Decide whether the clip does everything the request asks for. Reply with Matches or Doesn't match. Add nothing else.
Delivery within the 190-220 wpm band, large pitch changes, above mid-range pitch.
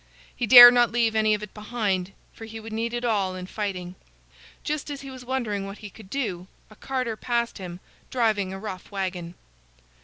Doesn't match